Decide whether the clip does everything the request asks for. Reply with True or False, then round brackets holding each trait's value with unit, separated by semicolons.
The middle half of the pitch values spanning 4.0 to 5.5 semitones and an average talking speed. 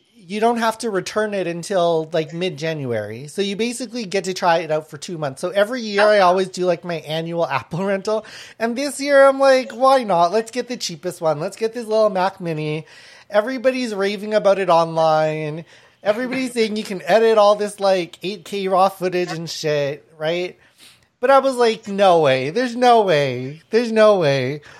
True (5.1 semitones; 195 wpm)